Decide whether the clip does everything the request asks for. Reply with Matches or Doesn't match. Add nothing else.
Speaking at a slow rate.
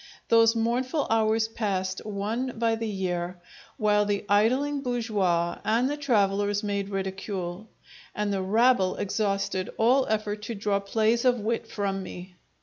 Doesn't match